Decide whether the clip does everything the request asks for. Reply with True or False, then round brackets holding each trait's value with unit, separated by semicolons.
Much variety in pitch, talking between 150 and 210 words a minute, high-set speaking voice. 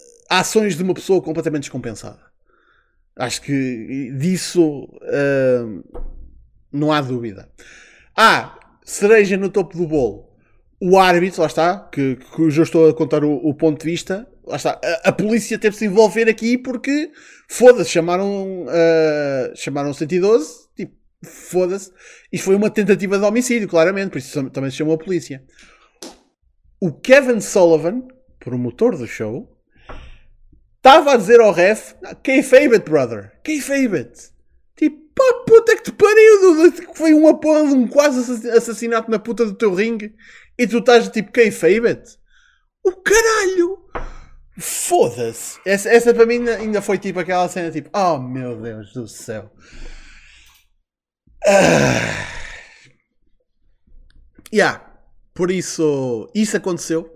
False (7.3 semitones; 140 wpm; 195 Hz)